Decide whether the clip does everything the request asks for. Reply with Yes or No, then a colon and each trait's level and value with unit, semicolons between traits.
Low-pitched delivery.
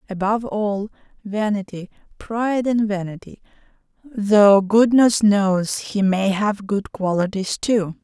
No: high, 205 Hz